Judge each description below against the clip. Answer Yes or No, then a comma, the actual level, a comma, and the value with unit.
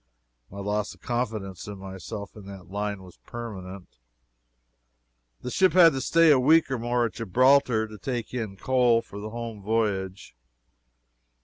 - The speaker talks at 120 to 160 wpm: Yes, average, 155 wpm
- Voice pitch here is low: Yes, low, 110 Hz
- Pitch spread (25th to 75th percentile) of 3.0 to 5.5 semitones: Yes, average, 4.0 semitones